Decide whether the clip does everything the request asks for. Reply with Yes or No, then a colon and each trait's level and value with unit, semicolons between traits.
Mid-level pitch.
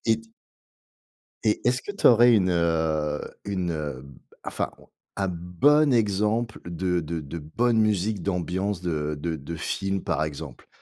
No: very low, 90 Hz